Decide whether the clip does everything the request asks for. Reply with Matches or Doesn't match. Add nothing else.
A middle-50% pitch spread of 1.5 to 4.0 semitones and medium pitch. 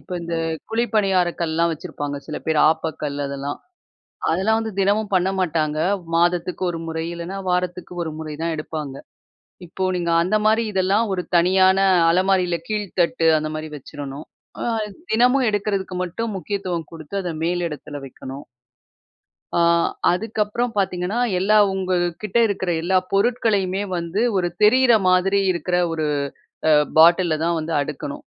Matches